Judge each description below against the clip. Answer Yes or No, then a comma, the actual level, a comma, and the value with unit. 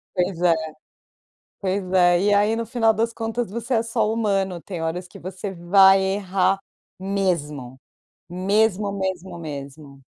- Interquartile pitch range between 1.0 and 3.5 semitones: Yes, average, 2.8 semitones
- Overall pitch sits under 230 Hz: Yes, high, 190 Hz